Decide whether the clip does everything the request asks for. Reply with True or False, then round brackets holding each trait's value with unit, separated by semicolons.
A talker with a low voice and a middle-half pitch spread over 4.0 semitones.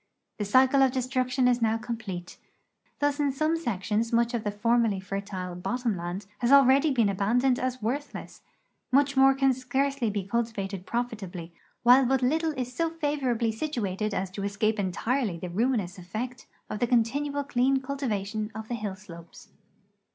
False (235 Hz; 4.5 semitones)